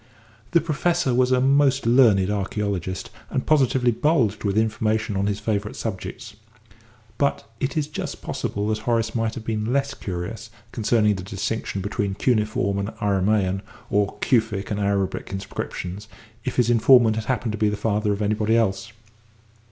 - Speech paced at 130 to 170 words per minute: Yes, average, 160 wpm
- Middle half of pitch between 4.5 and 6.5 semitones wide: No, average, 3.2 semitones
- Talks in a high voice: No, low, 110 Hz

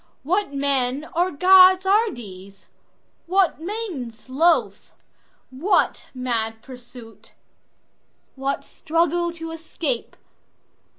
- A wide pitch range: Yes, wide, 6.1 semitones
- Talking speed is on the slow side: Yes, slow, 80 wpm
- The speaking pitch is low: No, very high, 285 Hz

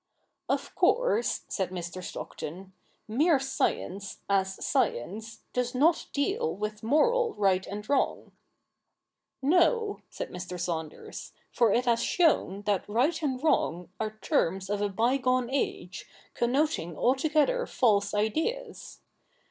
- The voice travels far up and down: Yes, wide, 7.5 semitones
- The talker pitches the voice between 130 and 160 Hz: No, high, 230 Hz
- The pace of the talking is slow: Yes, slow, 125 wpm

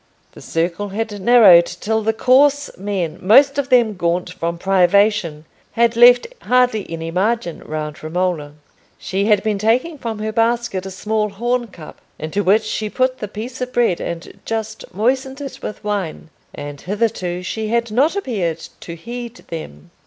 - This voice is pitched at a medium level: No, high, 210 Hz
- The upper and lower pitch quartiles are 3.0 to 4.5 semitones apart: No, average, 5.0 semitones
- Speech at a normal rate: Yes, average, 160 wpm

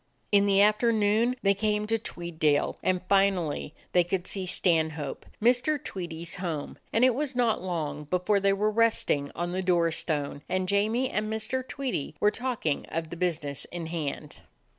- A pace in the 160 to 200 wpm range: Yes, average, 165 wpm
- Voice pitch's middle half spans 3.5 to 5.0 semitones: Yes, average, 4.7 semitones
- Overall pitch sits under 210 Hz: Yes, medium, 185 Hz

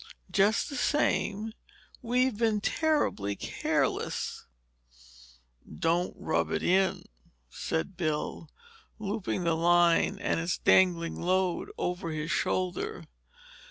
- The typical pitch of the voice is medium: Yes, medium, 180 Hz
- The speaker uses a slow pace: Yes, slow, 100 wpm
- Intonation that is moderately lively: Yes, average, 4.0 semitones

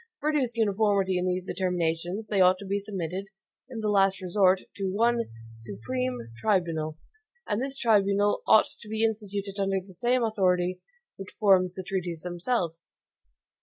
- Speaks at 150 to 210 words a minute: Yes, average, 155 wpm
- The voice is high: Yes, high, 195 Hz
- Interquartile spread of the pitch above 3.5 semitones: No, average, 2.9 semitones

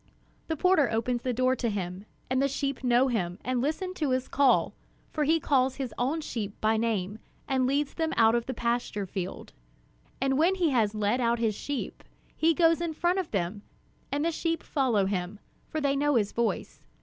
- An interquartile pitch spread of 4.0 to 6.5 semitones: Yes, average, 4.9 semitones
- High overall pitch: Yes, very high, 255 Hz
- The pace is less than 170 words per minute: No, average, 200 wpm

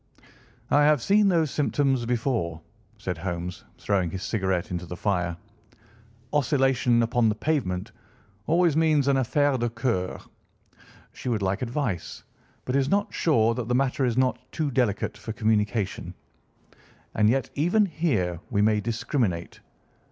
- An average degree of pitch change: No, wide, 6.1 semitones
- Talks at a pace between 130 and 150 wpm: Yes, average, 145 wpm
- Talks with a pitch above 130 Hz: No, low, 120 Hz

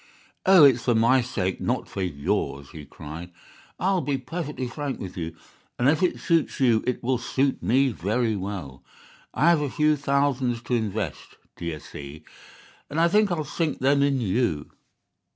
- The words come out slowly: No, average, 170 wpm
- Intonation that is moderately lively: No, wide, 7.2 semitones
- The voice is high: No, low, 125 Hz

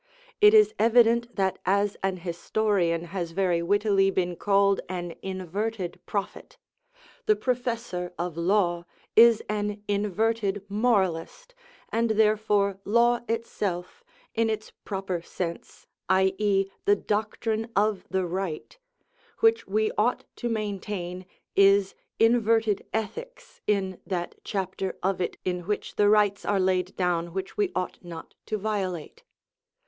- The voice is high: Yes, high, 200 Hz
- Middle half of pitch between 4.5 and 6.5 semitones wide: No, average, 3.1 semitones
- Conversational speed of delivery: No, slow, 125 wpm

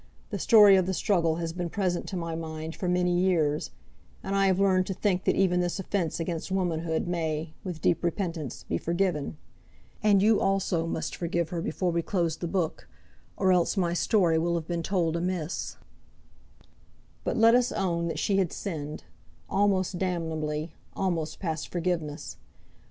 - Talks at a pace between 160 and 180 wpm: Yes, average, 170 wpm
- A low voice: No, medium, 175 Hz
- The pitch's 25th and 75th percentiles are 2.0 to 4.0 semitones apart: Yes, narrow, 2.6 semitones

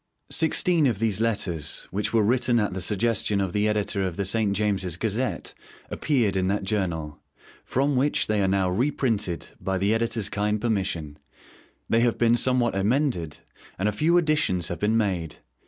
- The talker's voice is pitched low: Yes, low, 105 Hz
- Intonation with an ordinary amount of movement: Yes, average, 3.8 semitones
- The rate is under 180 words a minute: Yes, average, 170 wpm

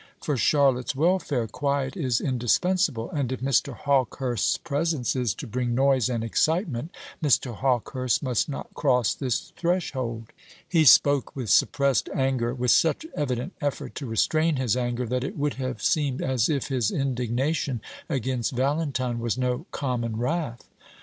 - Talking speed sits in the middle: Yes, average, 150 wpm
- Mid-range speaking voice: No, low, 130 Hz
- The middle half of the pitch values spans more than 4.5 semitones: No, average, 2.9 semitones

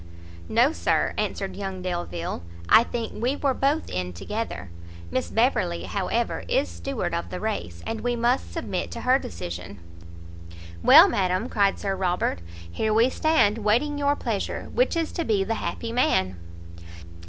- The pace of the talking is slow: No, average, 155 wpm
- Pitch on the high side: Yes, high, 210 Hz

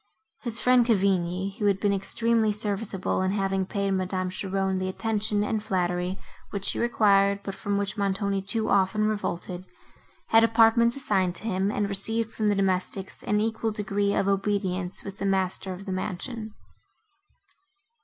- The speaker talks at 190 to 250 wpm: No, average, 160 wpm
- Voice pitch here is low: No, high, 200 Hz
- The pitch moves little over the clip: Yes, narrow, 2.1 semitones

